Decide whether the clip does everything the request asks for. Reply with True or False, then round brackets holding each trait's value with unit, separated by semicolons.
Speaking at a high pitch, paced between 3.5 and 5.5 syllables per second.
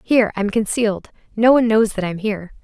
False (215 Hz; 6.4 syllables/s)